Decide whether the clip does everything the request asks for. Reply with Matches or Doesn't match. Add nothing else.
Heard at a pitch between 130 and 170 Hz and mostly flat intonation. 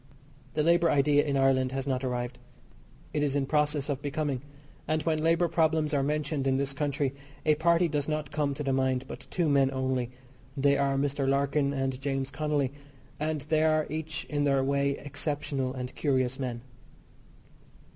Matches